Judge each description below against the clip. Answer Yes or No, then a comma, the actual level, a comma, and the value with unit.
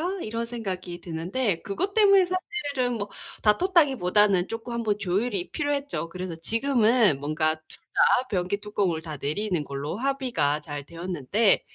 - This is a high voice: Yes, high, 205 Hz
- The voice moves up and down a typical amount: No, wide, 6.9 semitones